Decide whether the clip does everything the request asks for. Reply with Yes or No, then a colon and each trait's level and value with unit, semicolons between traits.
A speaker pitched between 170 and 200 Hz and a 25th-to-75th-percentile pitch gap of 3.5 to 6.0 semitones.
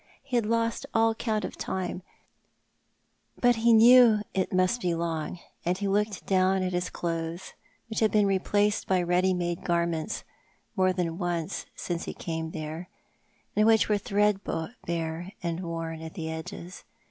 Yes: medium, 185 Hz; average, 3.8 semitones